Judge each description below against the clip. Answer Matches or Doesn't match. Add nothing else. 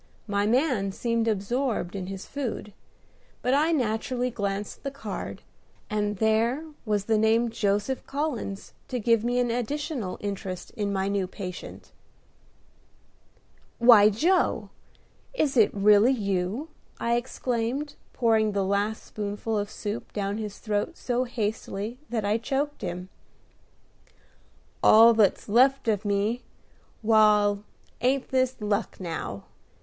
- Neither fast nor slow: Doesn't match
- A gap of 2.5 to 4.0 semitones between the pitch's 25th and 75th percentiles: Matches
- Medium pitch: Doesn't match